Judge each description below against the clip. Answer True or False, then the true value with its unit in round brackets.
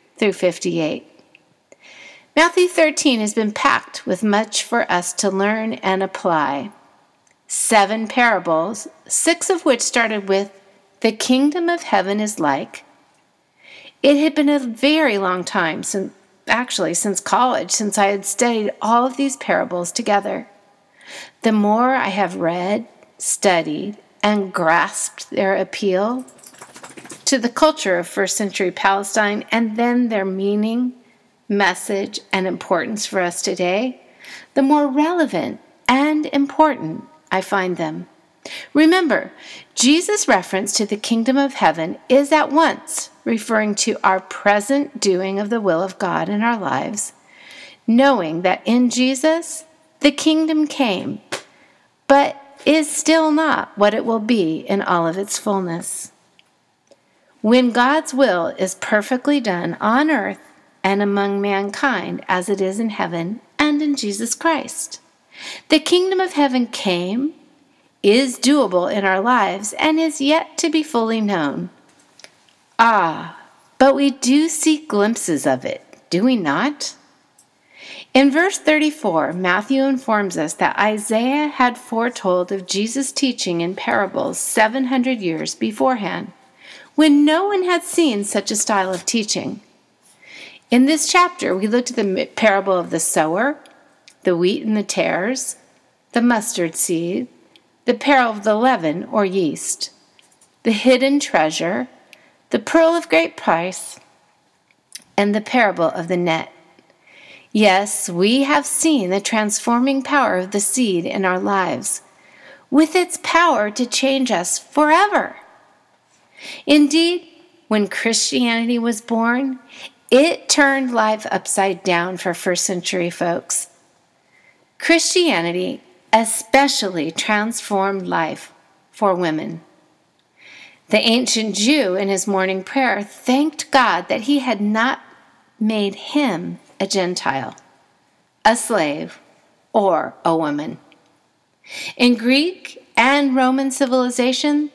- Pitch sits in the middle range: False (230 Hz)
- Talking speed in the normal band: False (130 wpm)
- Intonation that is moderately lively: False (6.2 semitones)